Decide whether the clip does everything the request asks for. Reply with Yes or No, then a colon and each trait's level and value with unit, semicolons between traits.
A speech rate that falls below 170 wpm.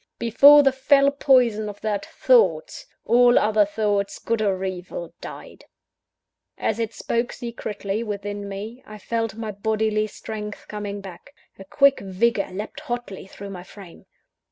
Yes: average, 145 wpm